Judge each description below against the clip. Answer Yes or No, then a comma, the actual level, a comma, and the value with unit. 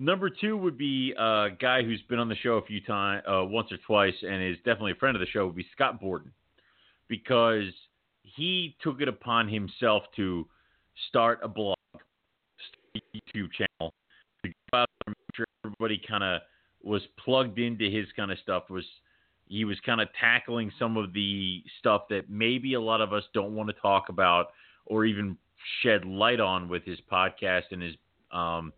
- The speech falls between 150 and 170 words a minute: No, average, 190 wpm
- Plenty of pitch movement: No, average, 3.7 semitones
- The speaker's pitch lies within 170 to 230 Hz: No, low, 105 Hz